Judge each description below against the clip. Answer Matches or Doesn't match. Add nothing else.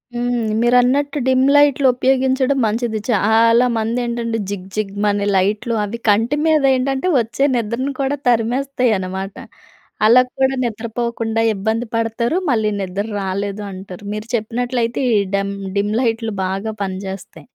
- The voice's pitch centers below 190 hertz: Doesn't match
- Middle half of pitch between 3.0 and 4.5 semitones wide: Matches